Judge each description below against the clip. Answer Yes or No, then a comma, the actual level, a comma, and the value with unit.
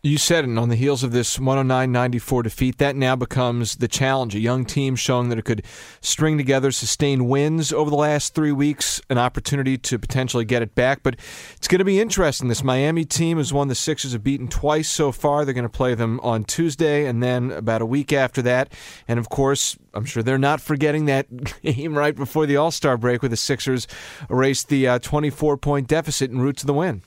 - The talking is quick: Yes, fast, 215 wpm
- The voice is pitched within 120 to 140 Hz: Yes, low, 135 Hz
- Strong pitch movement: No, average, 3.0 semitones